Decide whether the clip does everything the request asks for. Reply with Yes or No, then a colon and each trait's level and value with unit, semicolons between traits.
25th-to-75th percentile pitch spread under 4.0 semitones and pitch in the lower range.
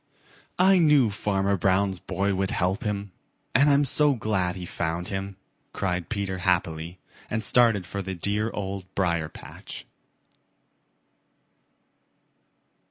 Yes: average, 2.9 semitones; low, 100 Hz